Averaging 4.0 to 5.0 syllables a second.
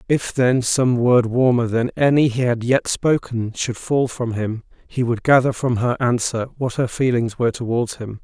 Yes: 4.6 syllables/s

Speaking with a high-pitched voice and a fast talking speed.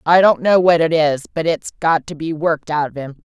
No: medium, 160 Hz; fast, 275 wpm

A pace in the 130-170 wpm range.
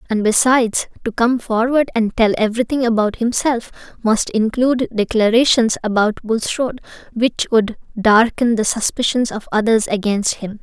Yes: slow, 135 wpm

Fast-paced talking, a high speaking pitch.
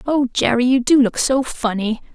No: average, 195 wpm; very high, 250 Hz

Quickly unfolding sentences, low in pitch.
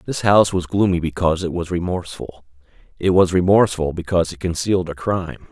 No: average, 175 wpm; very low, 90 Hz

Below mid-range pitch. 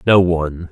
Yes: very low, 85 Hz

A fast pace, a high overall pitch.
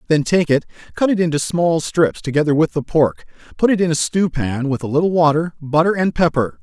No: fast, 225 wpm; medium, 155 Hz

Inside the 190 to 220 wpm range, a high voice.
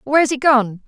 Yes: fast, 205 wpm; very high, 260 Hz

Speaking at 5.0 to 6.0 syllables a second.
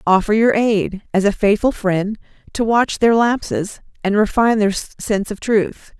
No: 4.4 syllables/s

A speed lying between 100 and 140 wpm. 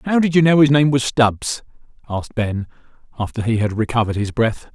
No: average, 200 wpm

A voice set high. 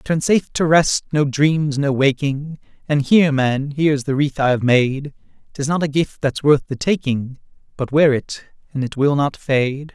No: medium, 145 Hz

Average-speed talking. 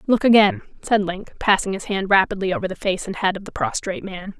No: fast, 230 wpm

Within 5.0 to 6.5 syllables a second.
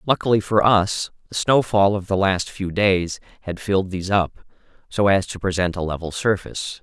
Yes: 5.1 syllables/s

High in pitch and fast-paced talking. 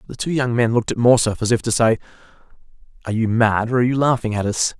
No: low, 115 Hz; fast, 240 wpm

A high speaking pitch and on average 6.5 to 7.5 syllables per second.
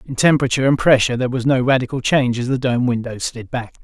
No: low, 125 Hz; 7.1 syllables/s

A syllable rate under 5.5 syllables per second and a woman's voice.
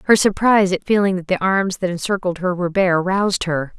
No: 5.8 syllables/s; female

